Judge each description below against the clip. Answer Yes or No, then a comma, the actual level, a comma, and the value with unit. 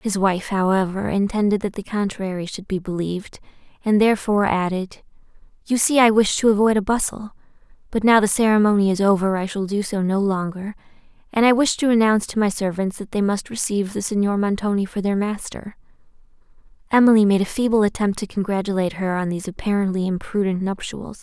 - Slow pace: No, average, 180 wpm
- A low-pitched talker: No, high, 200 Hz